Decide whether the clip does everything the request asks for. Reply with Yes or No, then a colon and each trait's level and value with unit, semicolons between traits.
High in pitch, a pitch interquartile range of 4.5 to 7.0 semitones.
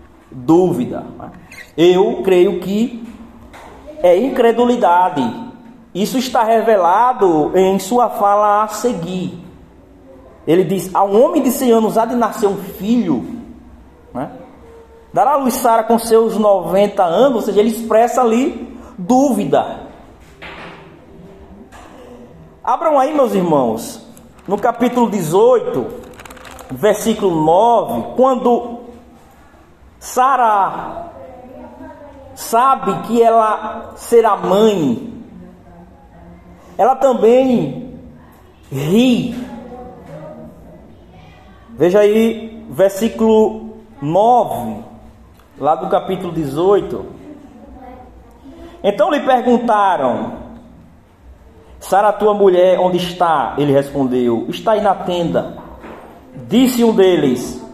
Yes: high, 215 Hz; average, 5.3 semitones